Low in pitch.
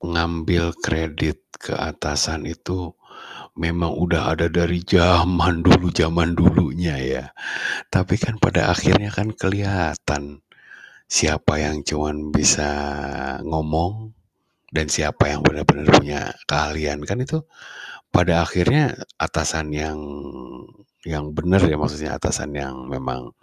Yes: very low, 80 Hz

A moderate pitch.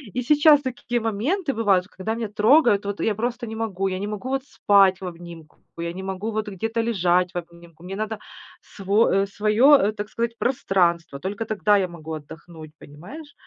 No: high, 205 Hz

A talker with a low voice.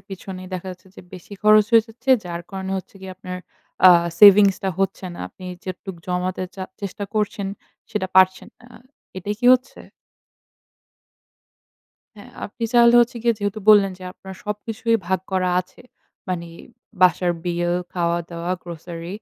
No: high, 190 Hz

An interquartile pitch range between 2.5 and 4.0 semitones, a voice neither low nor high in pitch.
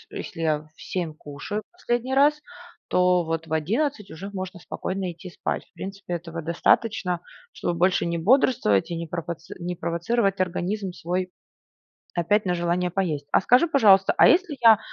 Yes: average, 3.7 semitones; medium, 180 Hz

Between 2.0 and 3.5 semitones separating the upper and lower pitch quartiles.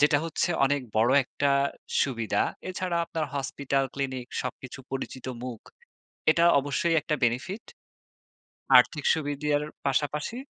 Yes: average, 2.8 semitones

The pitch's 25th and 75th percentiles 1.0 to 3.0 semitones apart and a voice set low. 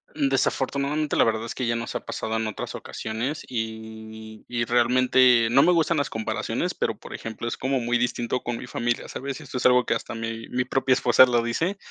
Yes: narrow, 2.4 semitones; low, 120 Hz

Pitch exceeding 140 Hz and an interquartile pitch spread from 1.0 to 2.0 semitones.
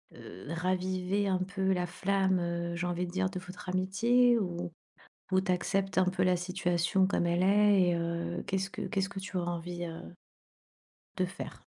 Yes: medium, 185 Hz; narrow, 1.7 semitones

